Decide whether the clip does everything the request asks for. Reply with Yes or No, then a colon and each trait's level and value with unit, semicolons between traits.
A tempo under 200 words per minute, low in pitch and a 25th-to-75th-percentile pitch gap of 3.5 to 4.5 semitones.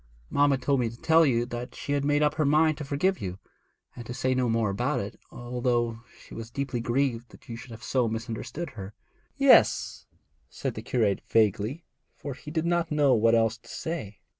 No: fast, 205 wpm; low, 125 Hz; average, 3.9 semitones